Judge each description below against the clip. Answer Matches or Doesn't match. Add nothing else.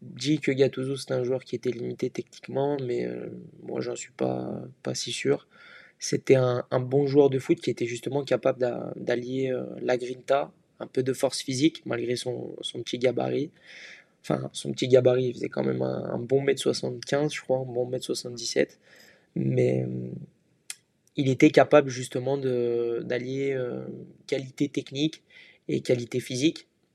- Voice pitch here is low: Matches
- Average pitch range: Doesn't match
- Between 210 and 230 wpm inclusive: Doesn't match